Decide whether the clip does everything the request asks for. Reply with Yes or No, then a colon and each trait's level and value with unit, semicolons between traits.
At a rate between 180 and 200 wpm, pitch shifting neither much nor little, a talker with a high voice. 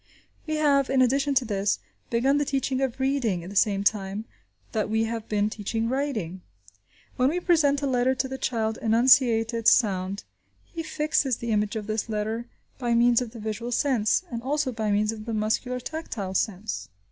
Yes: average, 195 wpm; average, 3.8 semitones; high, 235 Hz